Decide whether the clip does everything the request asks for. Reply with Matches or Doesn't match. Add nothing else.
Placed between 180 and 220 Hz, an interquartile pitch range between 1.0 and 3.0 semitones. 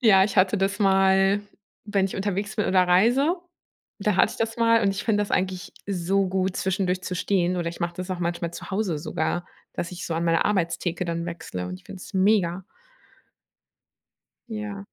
Matches